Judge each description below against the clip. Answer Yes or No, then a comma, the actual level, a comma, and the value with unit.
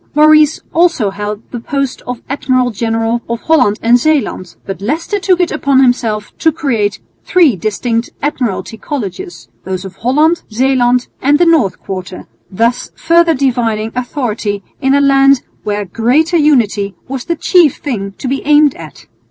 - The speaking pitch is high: Yes, very high, 250 Hz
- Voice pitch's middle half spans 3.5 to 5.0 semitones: No, wide, 5.6 semitones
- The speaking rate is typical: Yes, average, 155 wpm